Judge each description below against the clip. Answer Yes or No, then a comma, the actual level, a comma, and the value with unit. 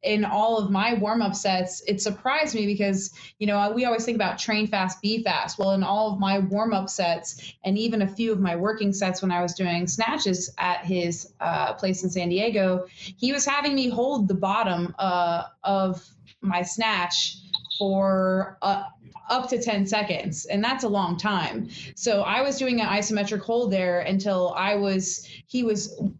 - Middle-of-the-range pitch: No, high, 195 Hz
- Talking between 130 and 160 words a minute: No, average, 190 wpm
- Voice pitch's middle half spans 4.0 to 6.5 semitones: No, average, 2.8 semitones